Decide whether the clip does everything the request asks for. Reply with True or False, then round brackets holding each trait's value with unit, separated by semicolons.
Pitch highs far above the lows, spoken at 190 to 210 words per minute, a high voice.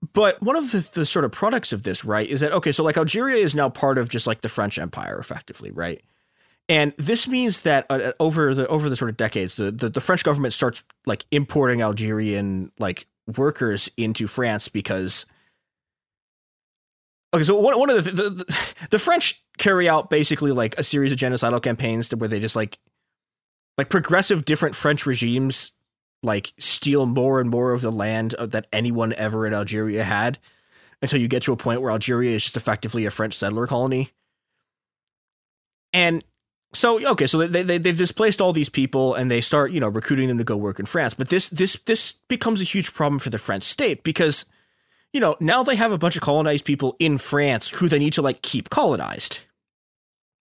False (6.1 semitones; 200 wpm; 135 Hz)